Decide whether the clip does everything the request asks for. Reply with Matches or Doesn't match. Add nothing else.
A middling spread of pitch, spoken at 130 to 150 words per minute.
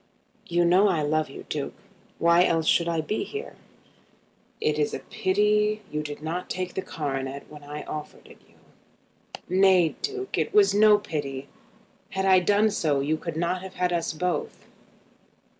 Doesn't match